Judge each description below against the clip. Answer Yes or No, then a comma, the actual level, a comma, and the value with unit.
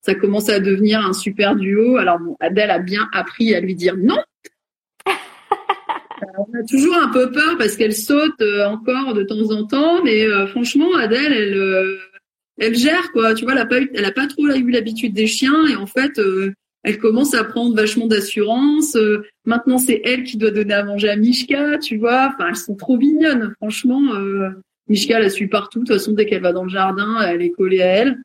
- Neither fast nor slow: No, fast, 225 wpm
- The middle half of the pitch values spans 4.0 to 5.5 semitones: Yes, average, 4.4 semitones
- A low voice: No, high, 225 Hz